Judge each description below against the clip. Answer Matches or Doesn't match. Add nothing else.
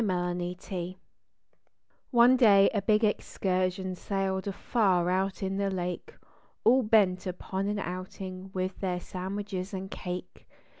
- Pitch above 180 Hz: Matches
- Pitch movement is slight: Matches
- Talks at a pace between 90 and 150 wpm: Matches